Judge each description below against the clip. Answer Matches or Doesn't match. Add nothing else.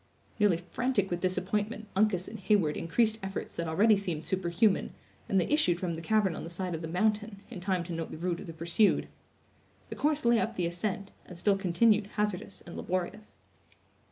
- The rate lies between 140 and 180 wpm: Doesn't match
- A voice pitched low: Doesn't match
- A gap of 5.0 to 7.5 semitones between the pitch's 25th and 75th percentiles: Doesn't match